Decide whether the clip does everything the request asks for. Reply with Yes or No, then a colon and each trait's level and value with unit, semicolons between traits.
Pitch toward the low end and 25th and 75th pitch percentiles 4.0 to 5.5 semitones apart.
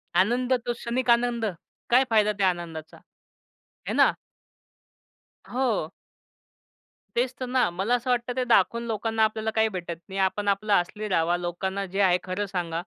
No: high, 210 Hz; average, 4.4 semitones